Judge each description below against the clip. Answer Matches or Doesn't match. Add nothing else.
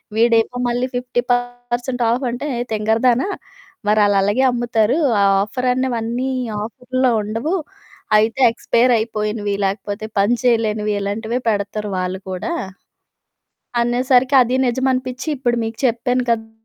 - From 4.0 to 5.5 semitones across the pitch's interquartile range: Doesn't match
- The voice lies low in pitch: Doesn't match